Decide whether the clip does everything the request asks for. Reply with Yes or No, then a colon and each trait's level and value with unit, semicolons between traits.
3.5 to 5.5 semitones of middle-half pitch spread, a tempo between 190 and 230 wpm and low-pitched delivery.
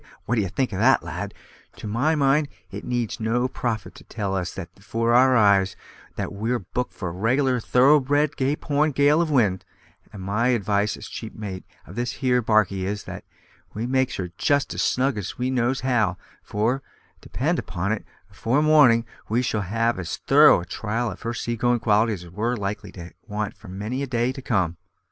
Yes: average, 4.1 semitones; average, 200 wpm; low, 115 Hz